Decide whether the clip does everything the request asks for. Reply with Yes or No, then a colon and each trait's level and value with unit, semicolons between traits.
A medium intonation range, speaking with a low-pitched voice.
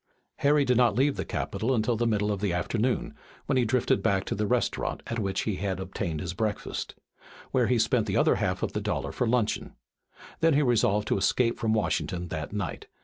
Yes: average, 4.0 semitones; low, 110 Hz